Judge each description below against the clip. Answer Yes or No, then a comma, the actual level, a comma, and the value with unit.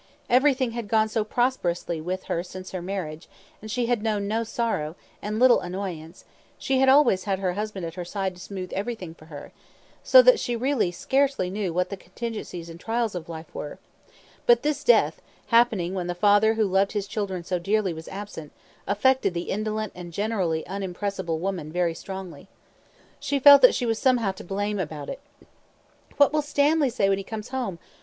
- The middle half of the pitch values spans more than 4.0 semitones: Yes, average, 4.7 semitones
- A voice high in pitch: Yes, high, 200 Hz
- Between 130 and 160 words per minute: No, average, 190 wpm